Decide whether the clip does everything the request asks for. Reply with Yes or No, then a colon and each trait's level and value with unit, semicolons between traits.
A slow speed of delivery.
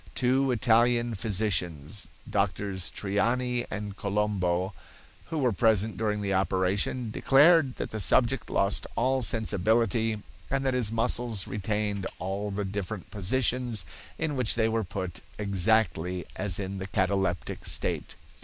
Yes: slow, 130 wpm